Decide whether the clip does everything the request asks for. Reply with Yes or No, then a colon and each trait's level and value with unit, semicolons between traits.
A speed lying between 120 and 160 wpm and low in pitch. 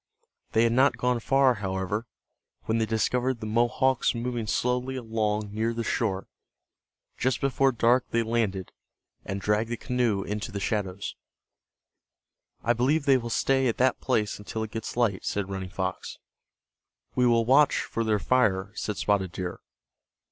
Yes: average, 155 wpm; low, 115 Hz